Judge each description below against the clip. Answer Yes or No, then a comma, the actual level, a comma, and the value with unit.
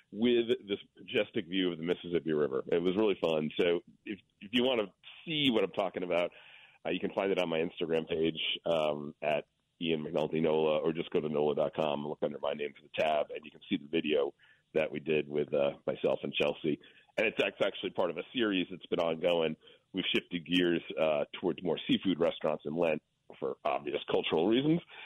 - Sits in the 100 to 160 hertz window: No, very low, 80 Hz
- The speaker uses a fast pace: Yes, fast, 210 wpm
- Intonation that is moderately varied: Yes, average, 3.4 semitones